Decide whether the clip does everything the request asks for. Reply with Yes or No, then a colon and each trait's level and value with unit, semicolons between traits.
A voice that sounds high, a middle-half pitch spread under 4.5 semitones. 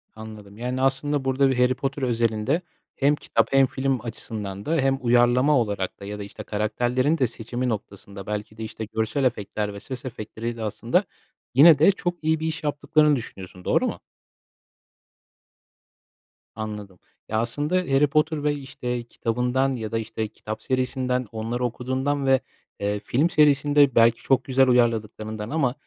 No: low, 125 Hz; average, 3.8 semitones